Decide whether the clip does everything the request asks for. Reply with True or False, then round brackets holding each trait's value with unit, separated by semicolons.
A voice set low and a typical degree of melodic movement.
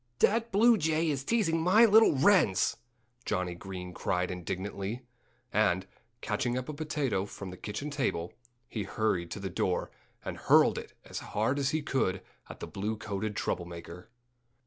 False (110 Hz; 8.6 semitones)